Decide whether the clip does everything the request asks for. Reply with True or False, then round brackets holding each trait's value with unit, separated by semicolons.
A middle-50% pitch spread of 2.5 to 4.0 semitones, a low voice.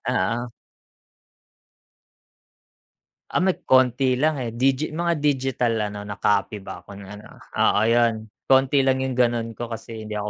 True (3.7 semitones; 120 Hz)